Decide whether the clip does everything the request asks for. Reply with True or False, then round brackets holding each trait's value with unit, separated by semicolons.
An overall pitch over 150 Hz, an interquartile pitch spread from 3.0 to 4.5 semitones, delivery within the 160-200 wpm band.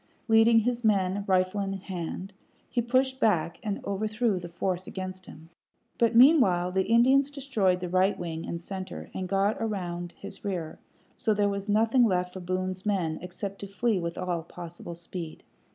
True (190 Hz; 3.5 semitones; 180 wpm)